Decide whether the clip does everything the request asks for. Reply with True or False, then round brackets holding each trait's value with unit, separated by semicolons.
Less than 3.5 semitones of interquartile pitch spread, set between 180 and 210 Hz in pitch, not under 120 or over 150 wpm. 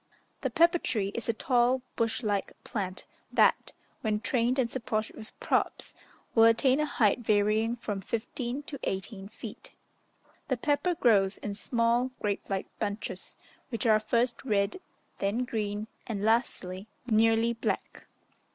False (2.9 semitones; 225 Hz; 140 wpm)